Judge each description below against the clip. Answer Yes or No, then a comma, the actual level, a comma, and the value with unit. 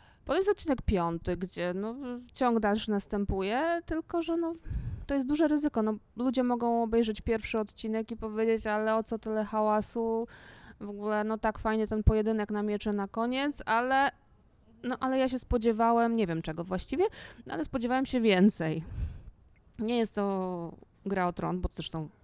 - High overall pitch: Yes, high, 225 Hz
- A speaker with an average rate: No, fast, 165 wpm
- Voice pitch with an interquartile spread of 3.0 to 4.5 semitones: Yes, average, 3.4 semitones